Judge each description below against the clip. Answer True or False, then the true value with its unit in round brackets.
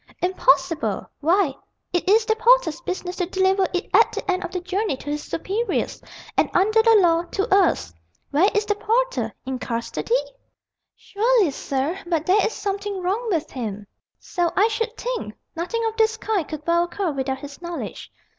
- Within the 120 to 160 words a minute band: False (175 wpm)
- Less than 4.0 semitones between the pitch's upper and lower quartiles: False (4.8 semitones)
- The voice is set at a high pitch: True (370 Hz)